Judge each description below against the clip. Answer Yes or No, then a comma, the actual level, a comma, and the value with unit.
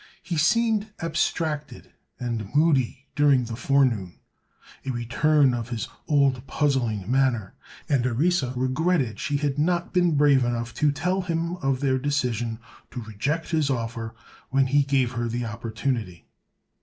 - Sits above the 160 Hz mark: No, low, 135 Hz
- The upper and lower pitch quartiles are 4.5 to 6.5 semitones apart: No, average, 4.1 semitones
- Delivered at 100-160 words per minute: Yes, slow, 135 wpm